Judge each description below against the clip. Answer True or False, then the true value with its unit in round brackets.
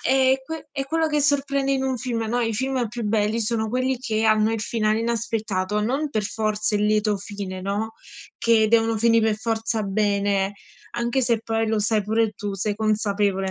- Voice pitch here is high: True (220 Hz)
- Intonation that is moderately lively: False (2.3 semitones)